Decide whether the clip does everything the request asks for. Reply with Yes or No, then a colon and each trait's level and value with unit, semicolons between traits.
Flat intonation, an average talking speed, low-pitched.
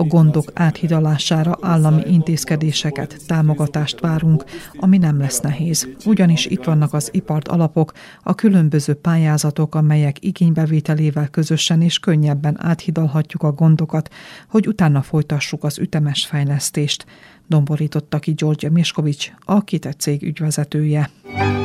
No: narrow, 1.9 semitones; average, 115 wpm; medium, 155 Hz